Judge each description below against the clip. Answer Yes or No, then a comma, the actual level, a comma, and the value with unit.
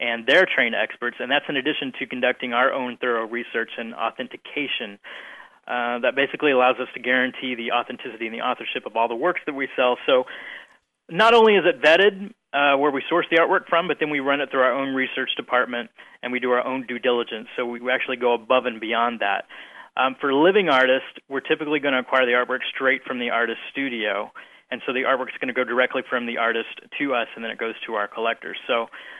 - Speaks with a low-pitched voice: Yes, low, 130 Hz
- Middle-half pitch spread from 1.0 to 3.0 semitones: Yes, average, 2.7 semitones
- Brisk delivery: Yes, fast, 230 wpm